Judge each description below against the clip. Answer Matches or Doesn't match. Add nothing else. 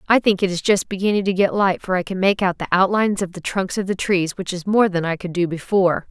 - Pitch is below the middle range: Doesn't match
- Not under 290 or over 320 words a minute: Matches